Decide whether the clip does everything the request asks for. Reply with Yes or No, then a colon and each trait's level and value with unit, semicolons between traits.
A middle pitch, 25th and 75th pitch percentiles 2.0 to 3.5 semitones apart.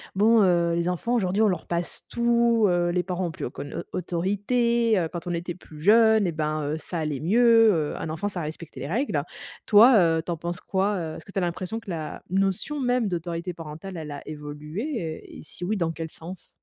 No: medium, 175 Hz; average, 4.4 semitones